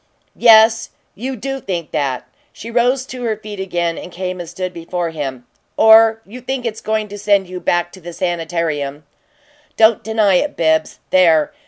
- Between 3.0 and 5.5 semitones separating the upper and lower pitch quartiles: Yes, average, 4.8 semitones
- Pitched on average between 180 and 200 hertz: Yes, high, 190 Hz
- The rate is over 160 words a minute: Yes, average, 175 wpm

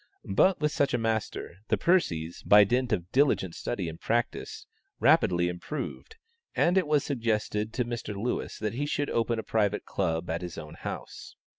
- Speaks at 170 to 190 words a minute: Yes, average, 175 wpm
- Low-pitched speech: Yes, low, 110 Hz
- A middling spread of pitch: No, wide, 7.7 semitones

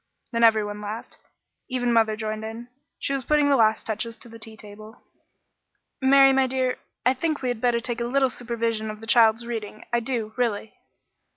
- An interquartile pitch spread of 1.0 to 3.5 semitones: Yes, narrow, 2.4 semitones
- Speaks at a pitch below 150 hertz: No, high, 230 Hz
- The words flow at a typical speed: Yes, average, 190 wpm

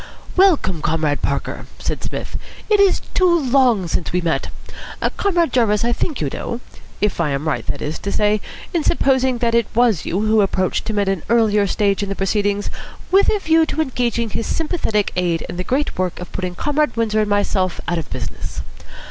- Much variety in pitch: Yes, wide, 5.9 semitones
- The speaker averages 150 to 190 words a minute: No, average, 200 wpm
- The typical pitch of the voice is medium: No, high, 215 Hz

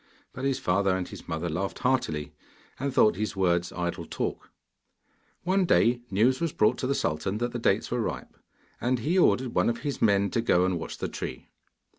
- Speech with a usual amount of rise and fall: No, wide, 5.8 semitones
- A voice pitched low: Yes, low, 110 Hz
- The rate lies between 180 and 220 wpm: Yes, average, 200 wpm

